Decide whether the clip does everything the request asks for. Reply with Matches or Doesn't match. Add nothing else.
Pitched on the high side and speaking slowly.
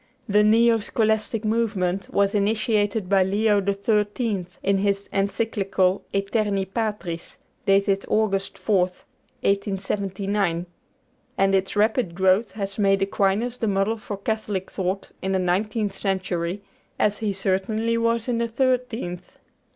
Matches